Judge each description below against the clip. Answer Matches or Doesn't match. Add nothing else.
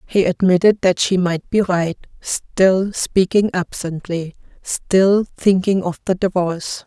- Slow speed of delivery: Matches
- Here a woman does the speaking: Matches